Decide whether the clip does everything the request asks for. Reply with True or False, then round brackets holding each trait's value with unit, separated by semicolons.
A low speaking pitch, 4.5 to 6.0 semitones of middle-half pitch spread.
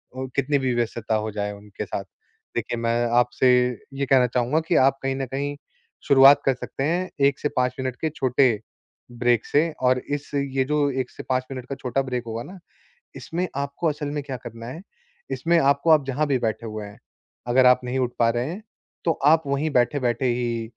False (130 Hz; 2.9 semitones)